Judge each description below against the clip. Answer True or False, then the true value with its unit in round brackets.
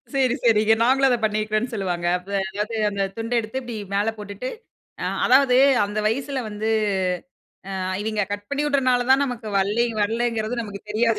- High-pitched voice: True (225 Hz)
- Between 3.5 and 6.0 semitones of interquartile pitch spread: False (3.0 semitones)